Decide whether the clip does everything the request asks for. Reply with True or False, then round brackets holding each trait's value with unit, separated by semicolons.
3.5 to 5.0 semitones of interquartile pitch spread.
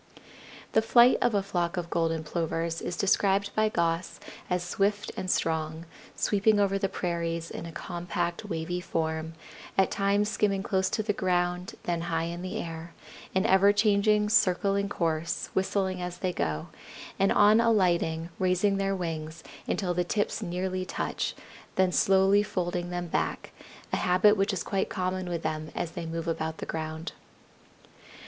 False (2.9 semitones)